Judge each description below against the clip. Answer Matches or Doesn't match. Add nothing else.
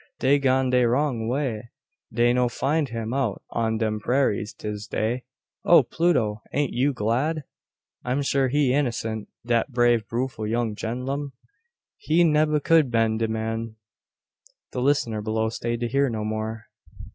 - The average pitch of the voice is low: Matches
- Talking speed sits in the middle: Matches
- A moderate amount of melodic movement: Matches